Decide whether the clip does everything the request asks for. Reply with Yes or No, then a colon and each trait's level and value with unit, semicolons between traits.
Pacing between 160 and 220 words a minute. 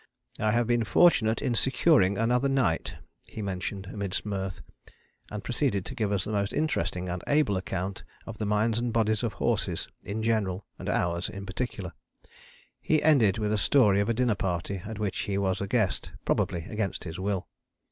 Yes: average, 185 wpm